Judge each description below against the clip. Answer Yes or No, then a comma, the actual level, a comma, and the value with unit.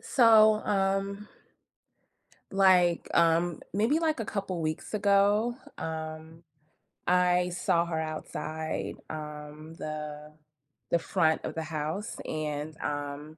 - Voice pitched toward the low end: No, medium, 170 Hz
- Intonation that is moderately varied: Yes, average, 4.1 semitones